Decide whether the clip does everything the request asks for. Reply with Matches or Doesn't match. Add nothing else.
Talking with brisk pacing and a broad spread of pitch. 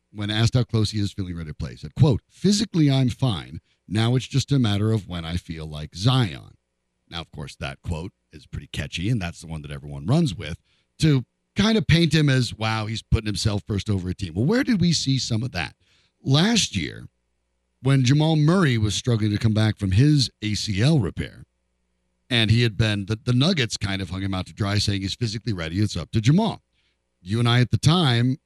Matches